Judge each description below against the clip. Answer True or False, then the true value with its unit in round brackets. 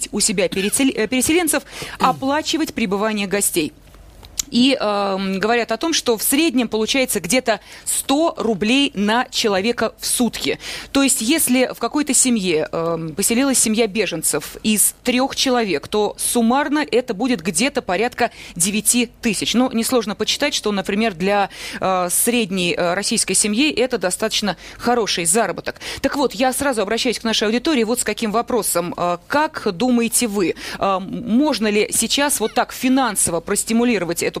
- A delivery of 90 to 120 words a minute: False (145 wpm)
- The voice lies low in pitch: False (230 Hz)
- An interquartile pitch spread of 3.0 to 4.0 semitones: True (3.7 semitones)